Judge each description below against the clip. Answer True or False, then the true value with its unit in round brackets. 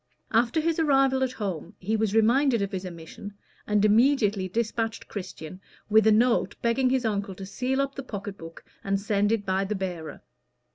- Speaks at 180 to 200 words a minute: True (185 wpm)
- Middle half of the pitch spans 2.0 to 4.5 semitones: True (4.2 semitones)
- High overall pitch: True (215 Hz)